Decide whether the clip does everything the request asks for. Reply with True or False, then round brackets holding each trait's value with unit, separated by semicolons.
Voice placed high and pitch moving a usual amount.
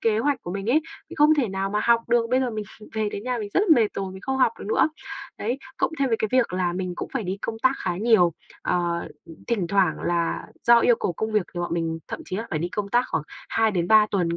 True (210 Hz; 4.6 semitones)